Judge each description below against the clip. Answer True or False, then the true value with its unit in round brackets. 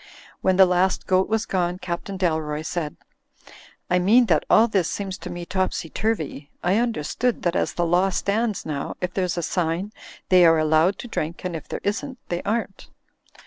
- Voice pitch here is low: False (180 Hz)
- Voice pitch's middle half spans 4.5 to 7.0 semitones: False (3.1 semitones)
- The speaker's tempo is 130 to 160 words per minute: False (190 wpm)